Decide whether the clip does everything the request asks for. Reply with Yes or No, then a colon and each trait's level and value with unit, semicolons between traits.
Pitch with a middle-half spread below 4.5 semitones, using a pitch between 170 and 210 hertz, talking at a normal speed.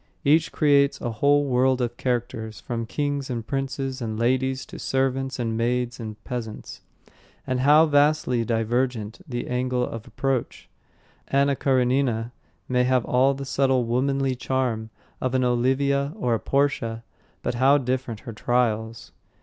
No: narrow, 2.4 semitones; low, 130 Hz; average, 145 wpm